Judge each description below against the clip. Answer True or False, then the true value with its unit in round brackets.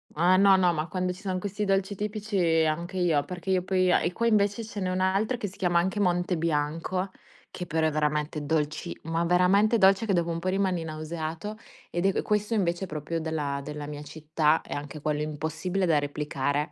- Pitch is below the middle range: False (175 Hz)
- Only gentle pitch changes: False (3.7 semitones)